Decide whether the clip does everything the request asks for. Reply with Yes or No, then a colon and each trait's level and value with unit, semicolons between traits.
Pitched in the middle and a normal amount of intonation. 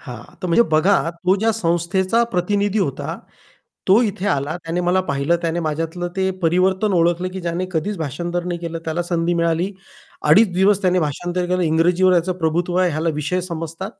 No: medium, 175 Hz; narrow, 2.2 semitones